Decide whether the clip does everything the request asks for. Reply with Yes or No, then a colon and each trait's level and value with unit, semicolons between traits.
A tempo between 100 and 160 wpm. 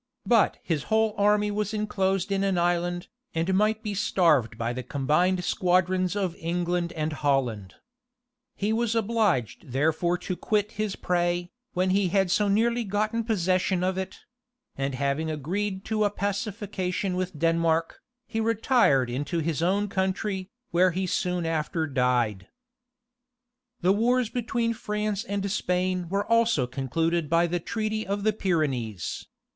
Yes: average, 145 wpm